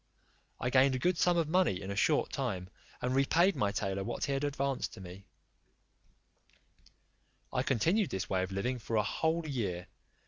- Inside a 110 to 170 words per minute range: No, average, 180 wpm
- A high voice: No, low, 125 Hz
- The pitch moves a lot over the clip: Yes, wide, 7.5 semitones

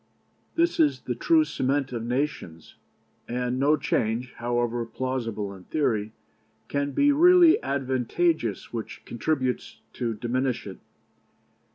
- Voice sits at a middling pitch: No, low, 125 Hz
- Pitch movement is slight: No, average, 4.0 semitones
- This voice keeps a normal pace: No, slow, 115 wpm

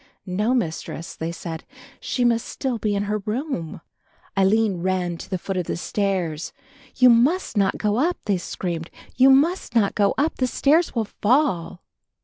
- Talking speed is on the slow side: No, average, 170 wpm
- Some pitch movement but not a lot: No, wide, 5.7 semitones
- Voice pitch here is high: Yes, high, 210 Hz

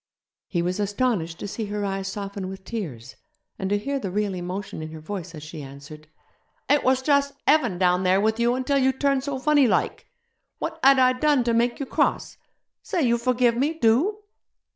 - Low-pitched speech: No, high, 220 Hz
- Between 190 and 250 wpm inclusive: Yes, average, 200 wpm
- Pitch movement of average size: No, wide, 5.9 semitones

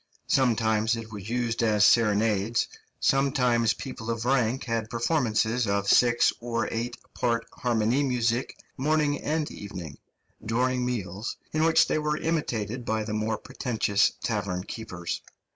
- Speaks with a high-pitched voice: No, low, 115 Hz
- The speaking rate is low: Yes, slow, 130 wpm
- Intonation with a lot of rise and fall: No, average, 2.7 semitones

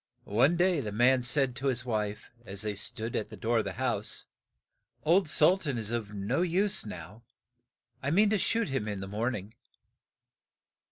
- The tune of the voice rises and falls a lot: Yes, wide, 6.1 semitones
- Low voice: Yes, low, 120 Hz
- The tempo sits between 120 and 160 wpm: No, average, 185 wpm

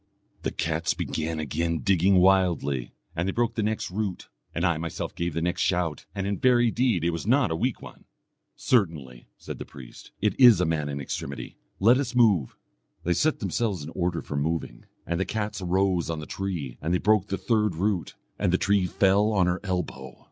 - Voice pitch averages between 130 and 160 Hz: No, very low, 90 Hz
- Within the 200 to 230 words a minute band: Yes, fast, 205 wpm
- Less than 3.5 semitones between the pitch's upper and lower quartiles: No, average, 4.0 semitones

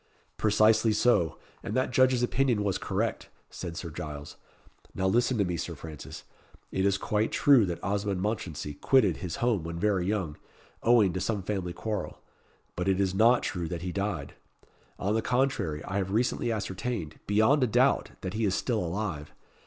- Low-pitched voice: Yes, low, 100 Hz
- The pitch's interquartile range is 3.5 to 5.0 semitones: Yes, average, 4.2 semitones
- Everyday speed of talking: Yes, average, 175 wpm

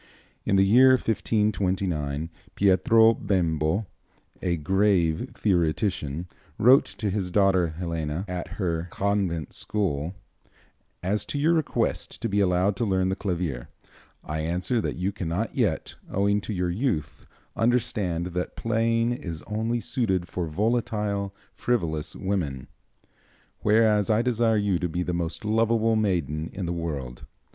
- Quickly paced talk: No, slow, 135 wpm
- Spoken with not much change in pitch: No, average, 4.3 semitones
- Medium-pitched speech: No, very low, 95 Hz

